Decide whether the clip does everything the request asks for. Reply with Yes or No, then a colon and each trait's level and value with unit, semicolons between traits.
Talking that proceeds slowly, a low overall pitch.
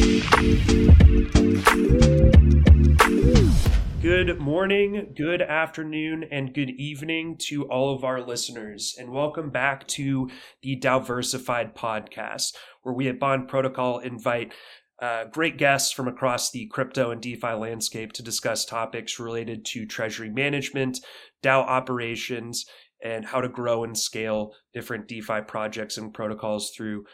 Yes: slow, 125 wpm; low, 125 Hz